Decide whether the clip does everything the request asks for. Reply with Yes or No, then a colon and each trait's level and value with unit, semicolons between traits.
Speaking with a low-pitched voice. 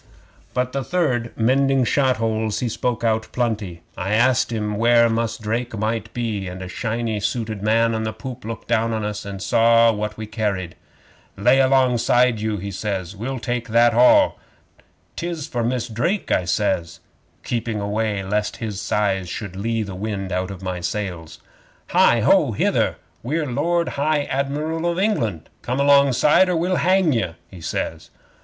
Yes: low, 115 Hz